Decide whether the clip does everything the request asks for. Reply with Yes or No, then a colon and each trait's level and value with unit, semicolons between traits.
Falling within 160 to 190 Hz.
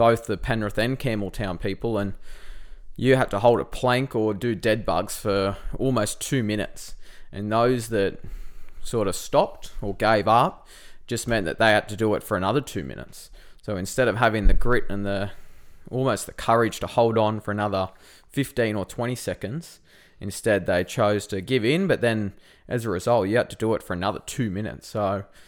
No: low, 110 Hz